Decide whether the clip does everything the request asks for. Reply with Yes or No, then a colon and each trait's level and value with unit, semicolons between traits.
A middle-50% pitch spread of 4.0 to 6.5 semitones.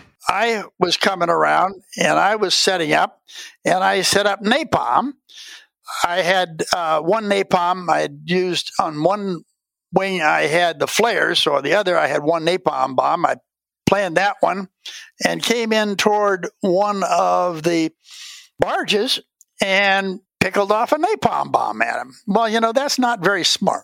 Yes: average, 4.3 semitones